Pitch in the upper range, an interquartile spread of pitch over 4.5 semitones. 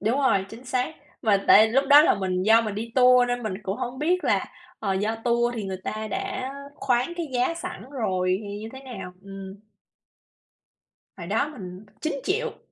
Yes: high, 230 Hz; average, 5.0 semitones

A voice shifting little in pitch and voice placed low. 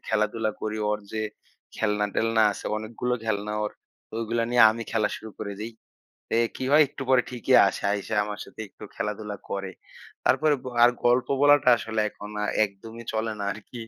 Yes: narrow, 2.0 semitones; low, 110 Hz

